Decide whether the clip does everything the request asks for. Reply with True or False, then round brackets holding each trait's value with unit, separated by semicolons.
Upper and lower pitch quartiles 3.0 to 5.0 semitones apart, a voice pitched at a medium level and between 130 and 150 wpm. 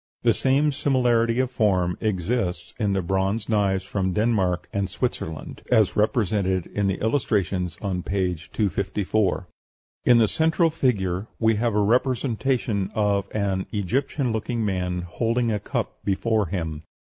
False (3.8 semitones; 105 Hz; 140 wpm)